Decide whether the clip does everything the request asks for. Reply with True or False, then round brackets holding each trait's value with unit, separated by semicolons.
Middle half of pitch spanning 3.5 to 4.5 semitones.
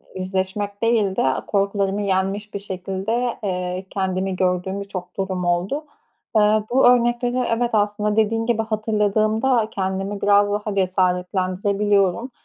False (2.4 semitones)